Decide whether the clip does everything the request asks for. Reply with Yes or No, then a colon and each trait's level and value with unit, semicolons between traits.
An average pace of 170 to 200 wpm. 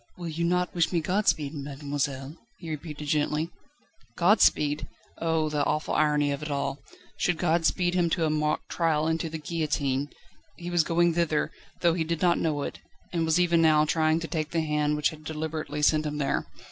Yes: average, 195 wpm